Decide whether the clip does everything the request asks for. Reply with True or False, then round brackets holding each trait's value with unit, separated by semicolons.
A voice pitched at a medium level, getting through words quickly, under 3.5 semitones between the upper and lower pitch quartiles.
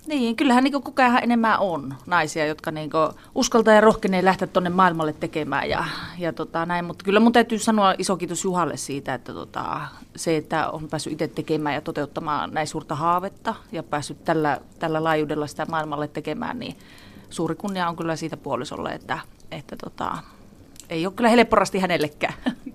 False (165 Hz; 170 wpm; 4.6 semitones)